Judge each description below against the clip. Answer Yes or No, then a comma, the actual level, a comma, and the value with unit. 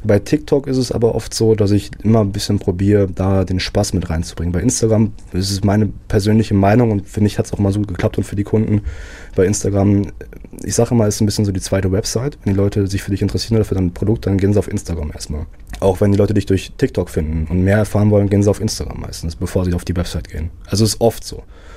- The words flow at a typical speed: No, fast, 260 wpm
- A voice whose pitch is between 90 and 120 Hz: Yes, low, 100 Hz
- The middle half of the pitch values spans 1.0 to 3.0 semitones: Yes, average, 2.7 semitones